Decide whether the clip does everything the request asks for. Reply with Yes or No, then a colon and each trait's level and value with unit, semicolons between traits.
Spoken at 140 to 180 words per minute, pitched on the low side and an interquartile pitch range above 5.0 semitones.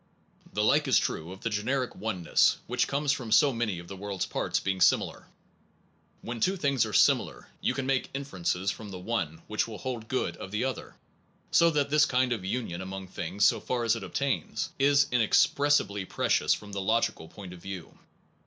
No: average, 200 wpm; low, 110 Hz; wide, 5.4 semitones